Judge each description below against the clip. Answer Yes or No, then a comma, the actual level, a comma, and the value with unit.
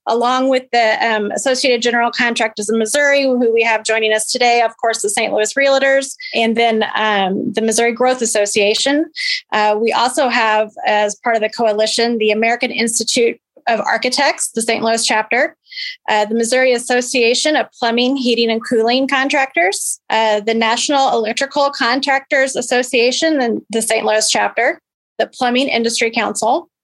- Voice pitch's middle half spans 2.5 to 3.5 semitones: Yes, average, 3.1 semitones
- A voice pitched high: Yes, high, 235 Hz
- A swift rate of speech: No, average, 160 wpm